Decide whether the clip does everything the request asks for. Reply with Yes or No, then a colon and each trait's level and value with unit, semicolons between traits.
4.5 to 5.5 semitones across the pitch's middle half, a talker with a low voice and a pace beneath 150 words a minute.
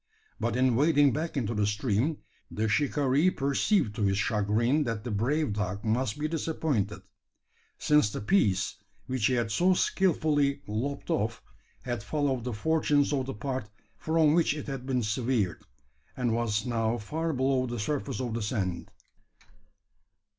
No: average, 5.2 semitones; low, 125 Hz; average, 155 wpm